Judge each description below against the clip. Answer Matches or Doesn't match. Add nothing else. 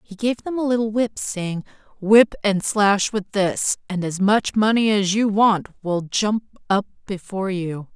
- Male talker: Doesn't match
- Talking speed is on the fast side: Doesn't match